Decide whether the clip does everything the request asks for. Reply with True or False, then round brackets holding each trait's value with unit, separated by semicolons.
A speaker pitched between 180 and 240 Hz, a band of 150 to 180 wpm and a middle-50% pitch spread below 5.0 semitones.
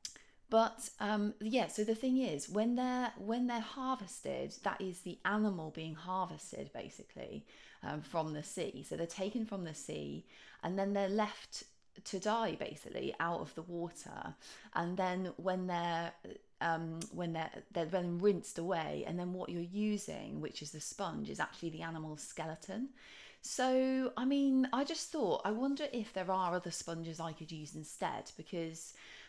False (190 Hz; 170 wpm; 5.3 semitones)